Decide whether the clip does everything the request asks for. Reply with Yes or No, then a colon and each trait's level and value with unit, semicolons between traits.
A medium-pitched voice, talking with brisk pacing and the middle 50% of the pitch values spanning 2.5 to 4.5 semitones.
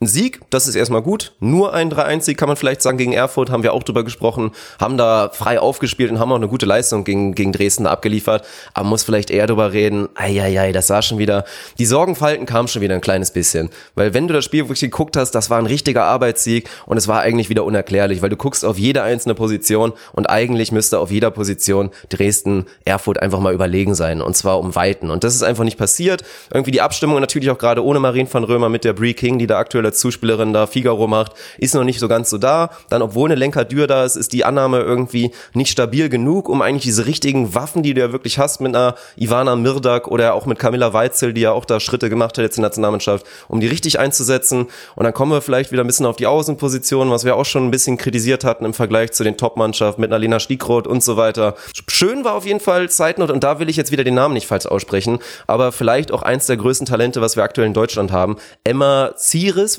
No: low, 120 Hz; fast, 245 wpm; average, 3.6 semitones